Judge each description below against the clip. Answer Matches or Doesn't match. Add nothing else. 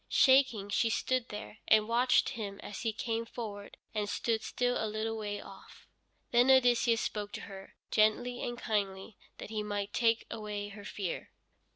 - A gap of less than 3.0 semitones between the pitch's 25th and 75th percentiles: Matches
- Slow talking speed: Doesn't match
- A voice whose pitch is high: Matches